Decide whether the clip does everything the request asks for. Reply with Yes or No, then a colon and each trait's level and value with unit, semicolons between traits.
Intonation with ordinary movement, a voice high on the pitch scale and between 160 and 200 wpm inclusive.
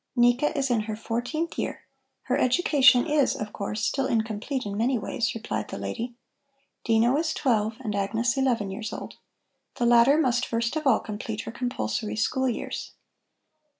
Yes: average, 3.2 semitones; high, 235 Hz; average, 165 wpm